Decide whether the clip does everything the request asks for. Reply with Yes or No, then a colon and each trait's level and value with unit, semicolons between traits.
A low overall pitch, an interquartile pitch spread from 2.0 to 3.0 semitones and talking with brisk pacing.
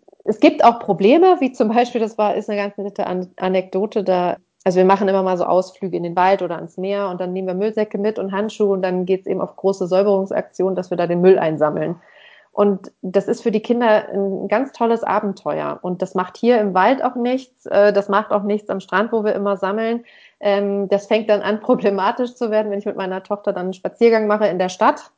No: high, 200 Hz; narrow, 2.5 semitones; fast, 230 wpm